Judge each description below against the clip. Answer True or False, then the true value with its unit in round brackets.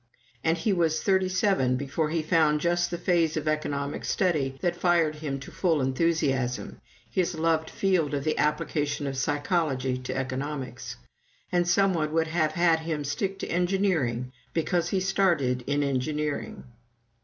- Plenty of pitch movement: False (3.6 semitones)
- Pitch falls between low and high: True (155 Hz)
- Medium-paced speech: True (160 wpm)